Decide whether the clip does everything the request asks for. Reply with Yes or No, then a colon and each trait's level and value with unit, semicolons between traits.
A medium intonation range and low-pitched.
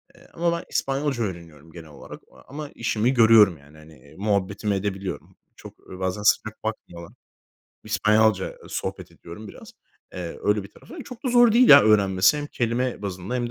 Yes: average, 5.0 semitones; low, 105 Hz